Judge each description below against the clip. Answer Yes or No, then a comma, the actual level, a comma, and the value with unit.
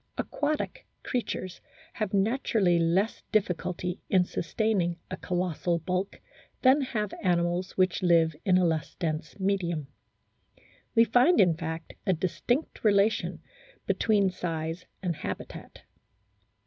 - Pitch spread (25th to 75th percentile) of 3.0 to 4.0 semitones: Yes, average, 3.6 semitones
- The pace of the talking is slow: Yes, slow, 115 wpm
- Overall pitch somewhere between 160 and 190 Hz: Yes, medium, 185 Hz